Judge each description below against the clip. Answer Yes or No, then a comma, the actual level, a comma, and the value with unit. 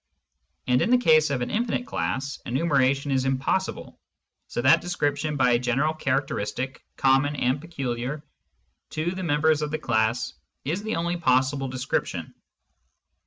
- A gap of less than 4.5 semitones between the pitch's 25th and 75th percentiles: Yes, average, 3.4 semitones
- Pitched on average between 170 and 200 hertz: No, medium, 140 Hz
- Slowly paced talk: No, average, 155 wpm